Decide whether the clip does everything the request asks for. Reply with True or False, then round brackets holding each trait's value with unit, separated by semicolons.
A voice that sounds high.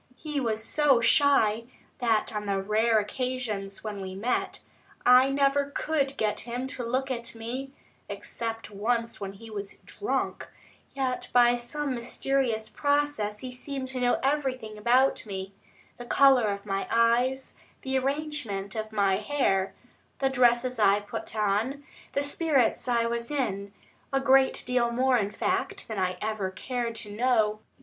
True (240 Hz)